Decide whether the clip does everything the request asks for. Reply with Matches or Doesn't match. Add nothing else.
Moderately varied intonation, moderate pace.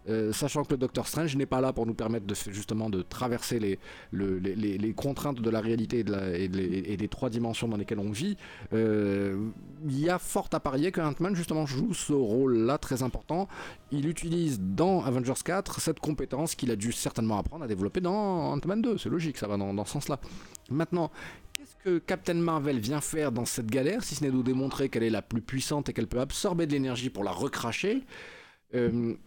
Doesn't match